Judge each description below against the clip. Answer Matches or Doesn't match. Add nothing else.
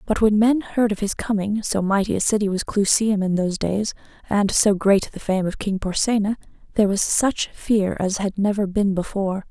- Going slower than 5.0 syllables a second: Doesn't match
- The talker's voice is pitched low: Doesn't match